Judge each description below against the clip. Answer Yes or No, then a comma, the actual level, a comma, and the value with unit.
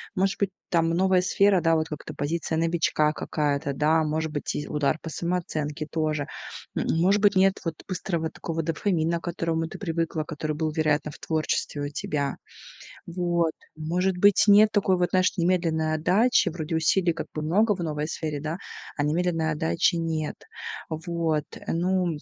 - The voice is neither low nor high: Yes, medium, 165 Hz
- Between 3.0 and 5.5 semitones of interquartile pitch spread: No, narrow, 2.6 semitones